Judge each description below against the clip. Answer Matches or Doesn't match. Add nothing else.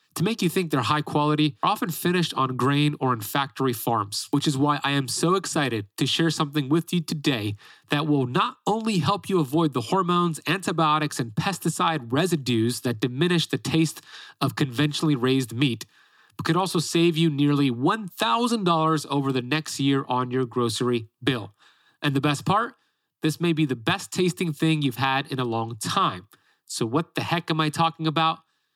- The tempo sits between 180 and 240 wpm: Matches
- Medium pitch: Matches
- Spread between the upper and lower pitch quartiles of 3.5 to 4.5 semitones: Matches